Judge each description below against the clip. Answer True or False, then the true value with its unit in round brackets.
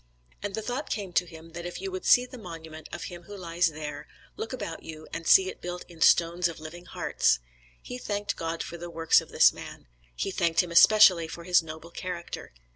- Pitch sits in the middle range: True (175 Hz)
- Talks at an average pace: False (220 wpm)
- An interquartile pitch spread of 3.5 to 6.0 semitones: False (2.4 semitones)